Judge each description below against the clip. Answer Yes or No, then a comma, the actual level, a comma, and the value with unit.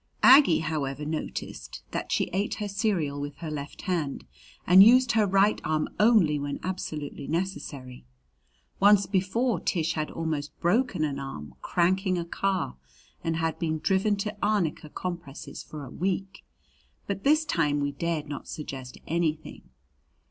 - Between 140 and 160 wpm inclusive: Yes, average, 150 wpm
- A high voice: No, medium, 170 Hz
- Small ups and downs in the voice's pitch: No, average, 4.8 semitones